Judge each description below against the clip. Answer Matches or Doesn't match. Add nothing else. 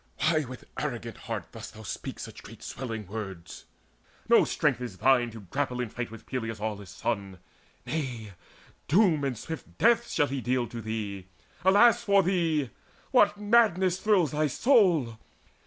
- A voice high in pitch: Doesn't match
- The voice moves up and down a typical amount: Doesn't match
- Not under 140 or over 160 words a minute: Matches